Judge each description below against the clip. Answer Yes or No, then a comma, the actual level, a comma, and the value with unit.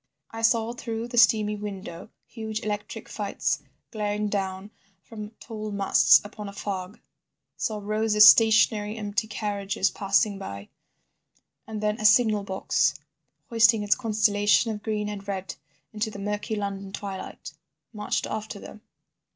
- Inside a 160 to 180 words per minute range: No, average, 140 wpm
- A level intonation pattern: Yes, narrow, 1.4 semitones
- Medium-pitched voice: No, high, 210 Hz